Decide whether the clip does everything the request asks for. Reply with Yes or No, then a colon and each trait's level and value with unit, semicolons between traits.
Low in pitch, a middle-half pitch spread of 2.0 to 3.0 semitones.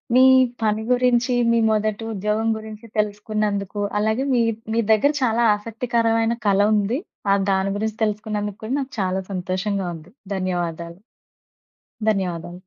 No: high, 210 Hz; average, 2.7 semitones